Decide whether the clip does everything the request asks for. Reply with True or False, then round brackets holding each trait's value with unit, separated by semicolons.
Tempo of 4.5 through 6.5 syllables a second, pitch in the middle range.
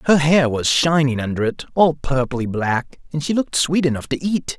True (5.0 syllables/s; 145 Hz)